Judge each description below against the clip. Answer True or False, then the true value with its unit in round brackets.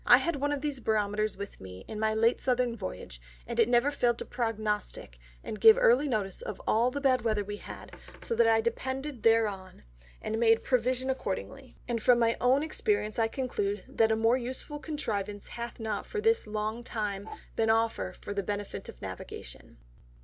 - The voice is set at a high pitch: True (225 Hz)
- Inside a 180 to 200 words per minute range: True (190 wpm)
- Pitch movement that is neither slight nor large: True (3.5 semitones)